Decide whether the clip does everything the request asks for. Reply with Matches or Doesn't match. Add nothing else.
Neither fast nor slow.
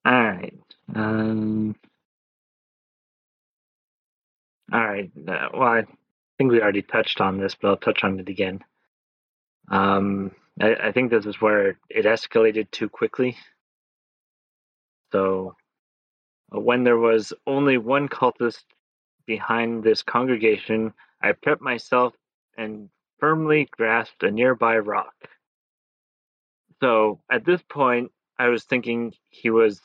Doesn't match